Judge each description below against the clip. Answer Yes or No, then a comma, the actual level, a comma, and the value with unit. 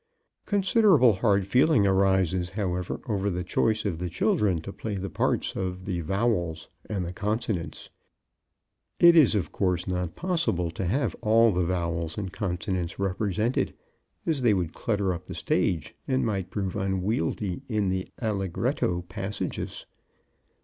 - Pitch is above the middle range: No, very low, 95 Hz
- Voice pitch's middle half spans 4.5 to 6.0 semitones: No, average, 3.5 semitones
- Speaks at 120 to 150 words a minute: Yes, average, 145 wpm